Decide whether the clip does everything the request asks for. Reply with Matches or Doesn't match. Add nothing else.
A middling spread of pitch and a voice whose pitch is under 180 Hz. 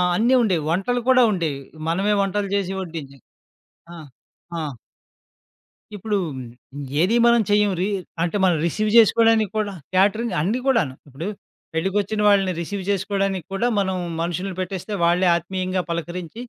Doesn't match